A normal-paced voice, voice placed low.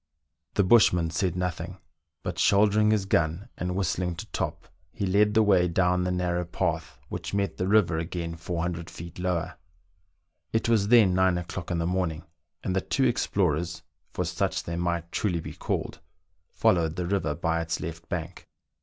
Yes: average, 170 wpm; very low, 90 Hz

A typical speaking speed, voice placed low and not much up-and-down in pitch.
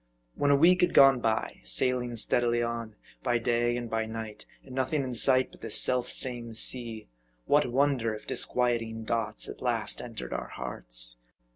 Yes: average, 170 wpm; low, 120 Hz; narrow, 2.3 semitones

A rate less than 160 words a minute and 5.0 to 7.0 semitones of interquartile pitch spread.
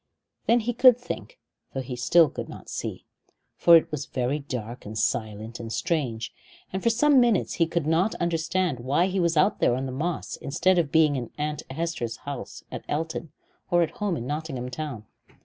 No: average, 195 wpm; wide, 5.5 semitones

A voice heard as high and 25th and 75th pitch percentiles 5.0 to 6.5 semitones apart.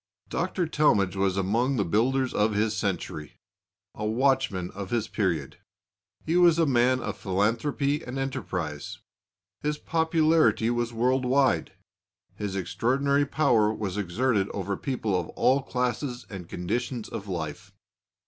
No: low, 120 Hz; wide, 5.5 semitones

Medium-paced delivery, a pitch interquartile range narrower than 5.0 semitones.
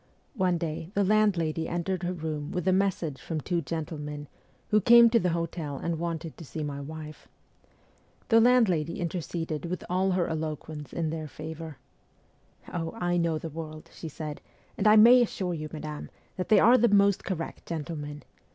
Yes: average, 180 wpm; average, 3.2 semitones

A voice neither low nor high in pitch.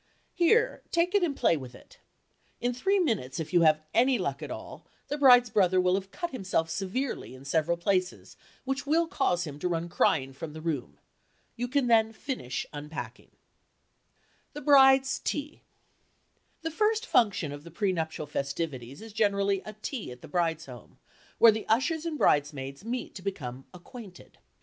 No: high, 195 Hz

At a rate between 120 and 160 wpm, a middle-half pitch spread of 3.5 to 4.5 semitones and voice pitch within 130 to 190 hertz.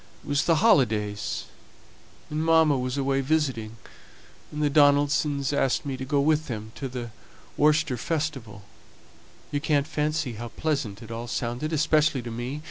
Yes: average, 155 wpm; average, 4.0 semitones; medium, 140 Hz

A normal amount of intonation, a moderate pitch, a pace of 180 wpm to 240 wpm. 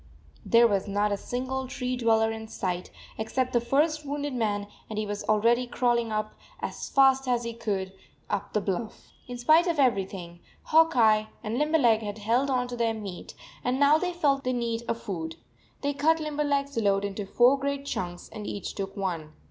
No: average, 4.8 semitones; high, 235 Hz; average, 190 wpm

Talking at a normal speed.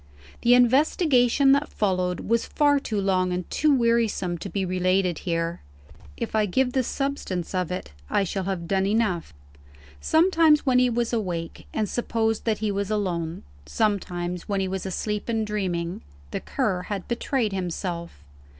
Yes: average, 160 wpm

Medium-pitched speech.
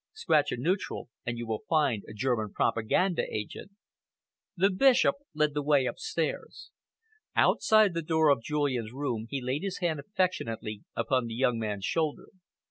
Yes: medium, 145 Hz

